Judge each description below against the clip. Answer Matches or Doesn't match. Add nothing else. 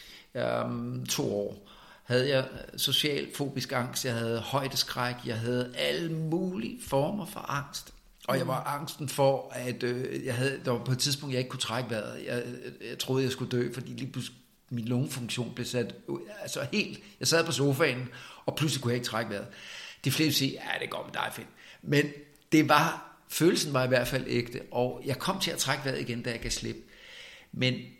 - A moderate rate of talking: Matches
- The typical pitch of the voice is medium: Doesn't match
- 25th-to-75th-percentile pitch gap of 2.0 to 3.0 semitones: Matches